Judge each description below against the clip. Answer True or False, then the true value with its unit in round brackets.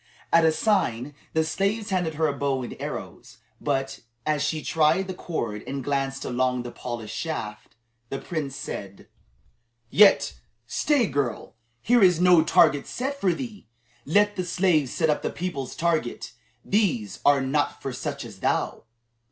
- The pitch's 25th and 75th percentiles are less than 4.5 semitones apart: False (5.2 semitones)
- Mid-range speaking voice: True (155 Hz)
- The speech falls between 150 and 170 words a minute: True (160 wpm)